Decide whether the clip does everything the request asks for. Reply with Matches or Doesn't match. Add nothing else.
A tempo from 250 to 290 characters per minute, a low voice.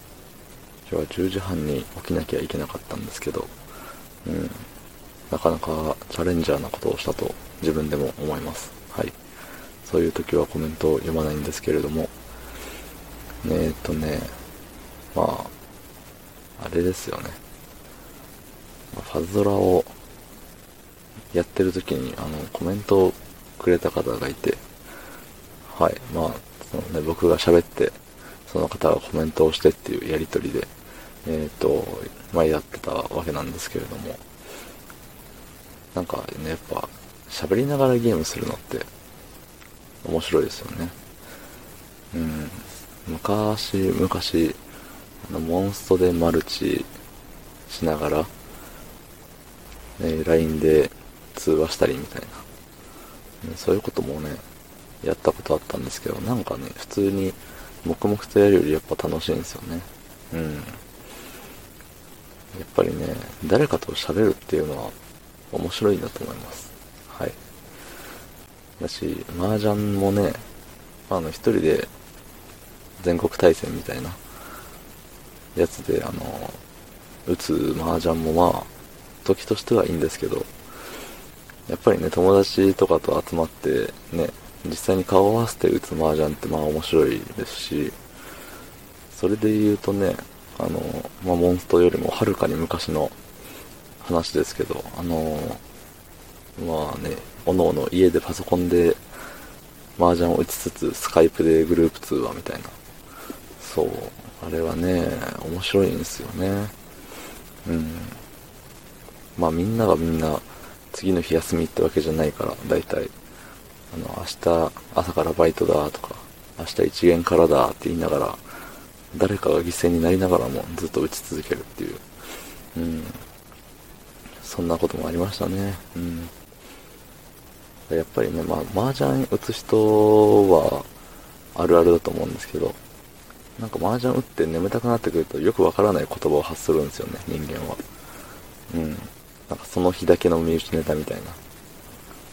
Matches